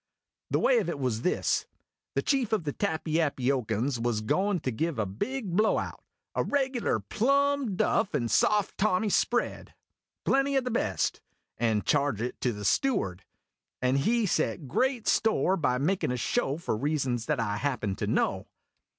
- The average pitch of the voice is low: No, medium, 155 Hz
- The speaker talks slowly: No, average, 170 wpm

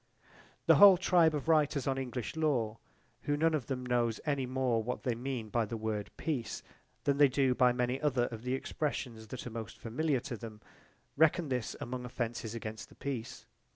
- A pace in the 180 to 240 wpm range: Yes, average, 190 wpm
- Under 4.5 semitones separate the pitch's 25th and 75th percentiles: Yes, average, 3.7 semitones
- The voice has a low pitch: Yes, low, 125 Hz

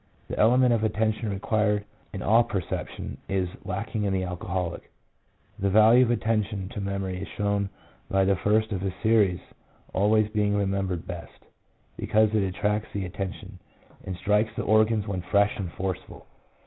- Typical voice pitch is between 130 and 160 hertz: No, low, 100 Hz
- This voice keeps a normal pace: Yes, average, 160 wpm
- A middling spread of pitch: No, narrow, 2.2 semitones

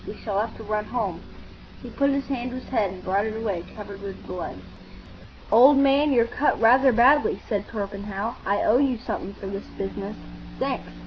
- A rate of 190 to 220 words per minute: Yes, average, 195 wpm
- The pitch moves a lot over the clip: No, average, 4.2 semitones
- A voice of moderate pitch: No, high, 220 Hz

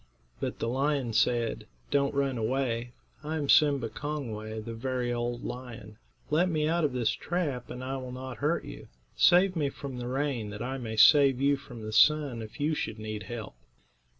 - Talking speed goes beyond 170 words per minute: Yes, average, 190 wpm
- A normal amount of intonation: Yes, average, 3.8 semitones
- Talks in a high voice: No, low, 130 Hz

